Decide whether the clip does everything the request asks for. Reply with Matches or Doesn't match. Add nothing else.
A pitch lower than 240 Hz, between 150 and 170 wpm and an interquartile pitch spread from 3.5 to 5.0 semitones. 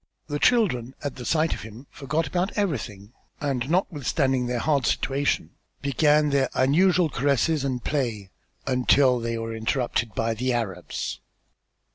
Doesn't match